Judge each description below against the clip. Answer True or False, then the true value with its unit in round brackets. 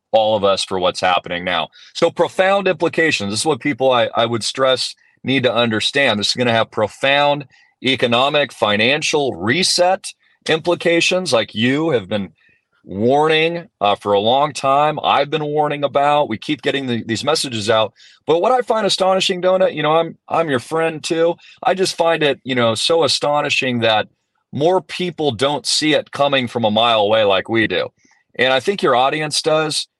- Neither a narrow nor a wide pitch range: False (5.7 semitones)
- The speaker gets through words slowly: False (185 wpm)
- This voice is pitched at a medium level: True (145 Hz)